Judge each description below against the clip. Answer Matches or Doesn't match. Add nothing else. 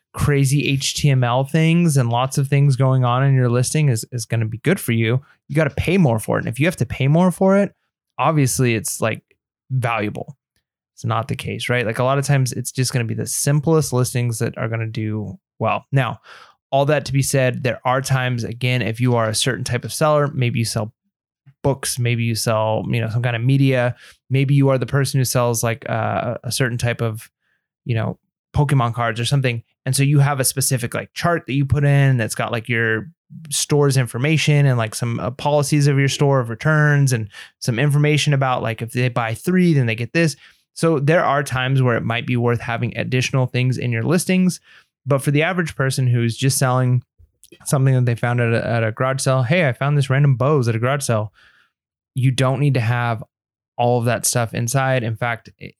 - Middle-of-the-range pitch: Doesn't match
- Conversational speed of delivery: Doesn't match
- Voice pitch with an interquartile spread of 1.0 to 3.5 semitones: Matches